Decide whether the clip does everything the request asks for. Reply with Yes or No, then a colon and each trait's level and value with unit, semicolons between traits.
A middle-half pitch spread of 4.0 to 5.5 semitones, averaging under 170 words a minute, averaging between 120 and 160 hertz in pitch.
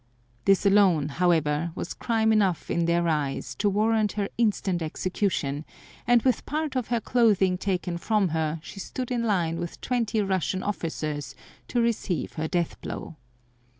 No: average, 4.8 semitones; average, 155 wpm; high, 190 Hz